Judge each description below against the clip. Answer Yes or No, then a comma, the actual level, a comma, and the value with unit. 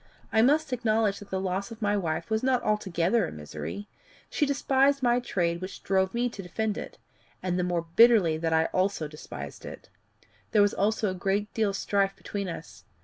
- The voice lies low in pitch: No, high, 200 Hz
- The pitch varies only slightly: No, average, 4.0 semitones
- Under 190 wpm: No, average, 200 wpm